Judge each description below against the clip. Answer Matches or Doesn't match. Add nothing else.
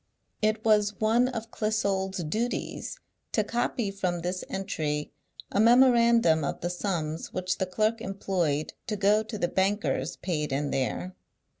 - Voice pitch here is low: Doesn't match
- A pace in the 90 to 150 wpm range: Matches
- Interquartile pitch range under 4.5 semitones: Matches